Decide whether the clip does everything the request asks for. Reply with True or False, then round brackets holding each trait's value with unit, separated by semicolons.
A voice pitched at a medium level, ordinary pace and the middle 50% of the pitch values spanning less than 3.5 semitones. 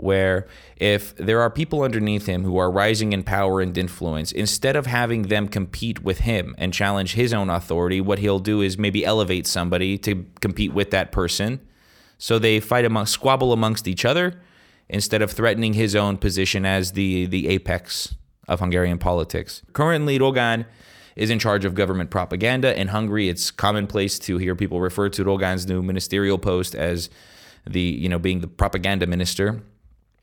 False (100 Hz; 175 wpm; 2.9 semitones)